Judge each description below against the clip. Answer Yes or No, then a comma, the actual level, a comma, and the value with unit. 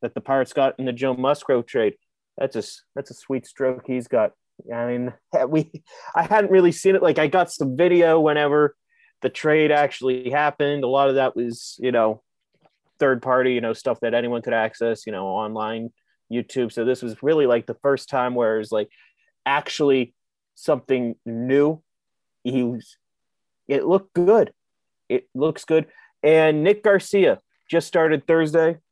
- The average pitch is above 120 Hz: Yes, low, 135 Hz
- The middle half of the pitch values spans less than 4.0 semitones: No, average, 4.8 semitones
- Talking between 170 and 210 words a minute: Yes, average, 175 wpm